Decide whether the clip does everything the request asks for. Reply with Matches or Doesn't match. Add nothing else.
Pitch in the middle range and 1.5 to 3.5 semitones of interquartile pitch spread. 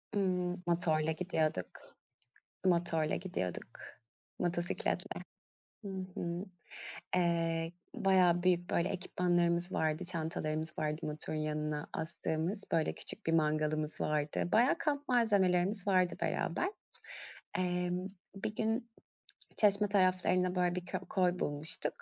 Matches